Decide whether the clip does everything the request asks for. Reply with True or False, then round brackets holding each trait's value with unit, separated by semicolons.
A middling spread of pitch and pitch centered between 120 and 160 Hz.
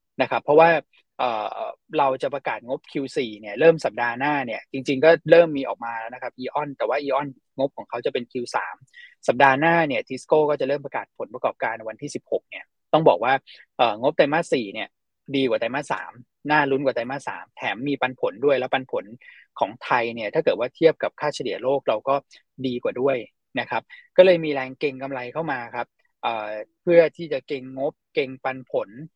True (4.0 semitones; 140 Hz)